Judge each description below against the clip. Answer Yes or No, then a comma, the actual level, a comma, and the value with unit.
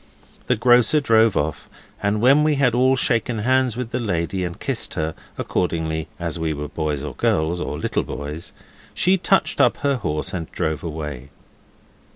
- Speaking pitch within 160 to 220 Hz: No, very low, 90 Hz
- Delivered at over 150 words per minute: Yes, average, 175 wpm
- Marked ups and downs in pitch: Yes, wide, 7.9 semitones